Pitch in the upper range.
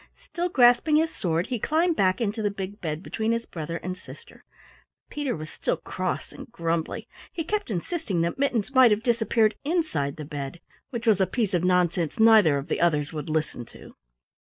Yes: high, 200 Hz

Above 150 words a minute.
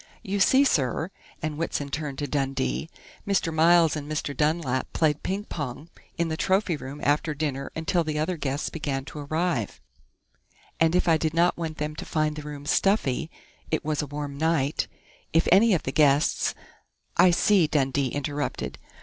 Yes: average, 175 wpm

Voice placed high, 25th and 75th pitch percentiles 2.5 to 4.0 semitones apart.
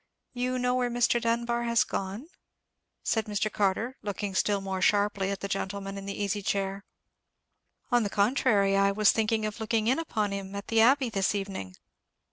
Yes: high, 210 Hz; average, 2.9 semitones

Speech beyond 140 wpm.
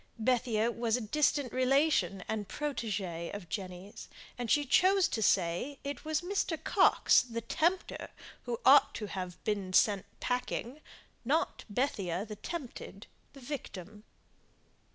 No: slow, 135 wpm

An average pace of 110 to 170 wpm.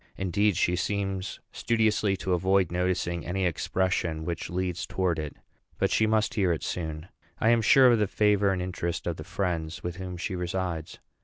No: average, 180 wpm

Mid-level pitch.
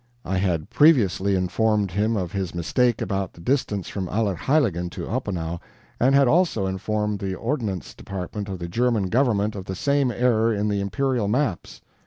No: low, 105 Hz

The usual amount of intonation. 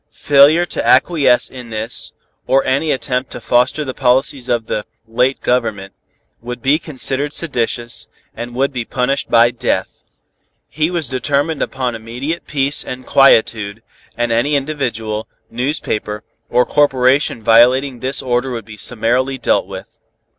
Yes: average, 3.0 semitones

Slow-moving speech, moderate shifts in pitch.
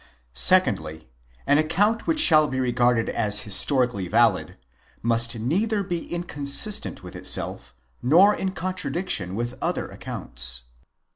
No: slow, 120 wpm; wide, 8.4 semitones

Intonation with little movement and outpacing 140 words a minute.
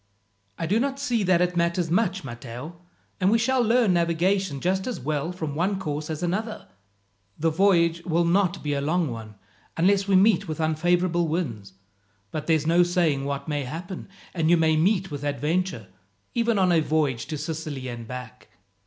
No: average, 3.9 semitones; average, 180 wpm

